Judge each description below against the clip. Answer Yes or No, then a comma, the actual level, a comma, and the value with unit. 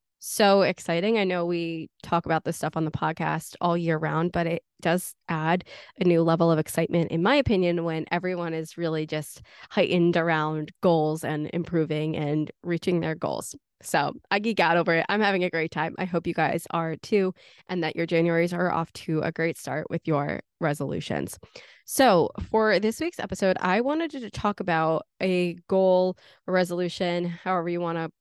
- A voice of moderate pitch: Yes, medium, 170 Hz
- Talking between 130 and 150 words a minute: No, average, 190 wpm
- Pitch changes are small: Yes, narrow, 2.3 semitones